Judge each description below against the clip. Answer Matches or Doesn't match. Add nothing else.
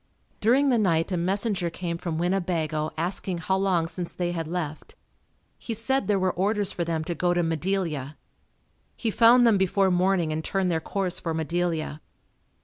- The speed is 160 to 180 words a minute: Matches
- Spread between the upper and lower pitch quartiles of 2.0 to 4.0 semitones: Matches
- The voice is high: Doesn't match